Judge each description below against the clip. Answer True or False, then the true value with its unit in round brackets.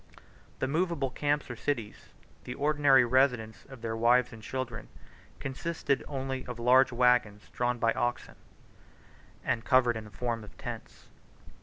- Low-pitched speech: True (125 Hz)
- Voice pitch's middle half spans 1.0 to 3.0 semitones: True (2.5 semitones)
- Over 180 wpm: False (145 wpm)